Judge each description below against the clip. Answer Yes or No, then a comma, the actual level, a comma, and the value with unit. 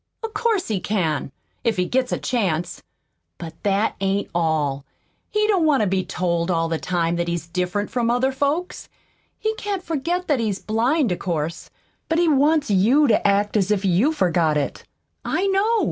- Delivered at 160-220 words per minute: Yes, average, 185 wpm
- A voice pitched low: No, high, 210 Hz